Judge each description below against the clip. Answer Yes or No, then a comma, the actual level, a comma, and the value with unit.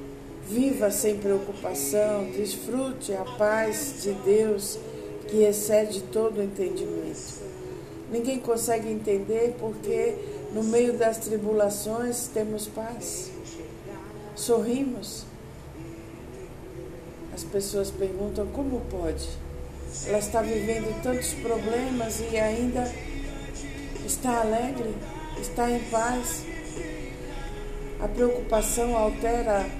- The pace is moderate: No, slow, 90 wpm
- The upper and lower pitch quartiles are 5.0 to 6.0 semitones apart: No, narrow, 2.5 semitones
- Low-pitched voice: No, high, 220 Hz